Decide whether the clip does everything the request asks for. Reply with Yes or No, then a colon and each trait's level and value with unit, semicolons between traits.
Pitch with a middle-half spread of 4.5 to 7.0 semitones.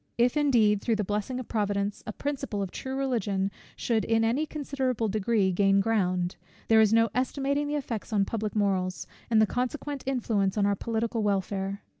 No: average, 4.0 semitones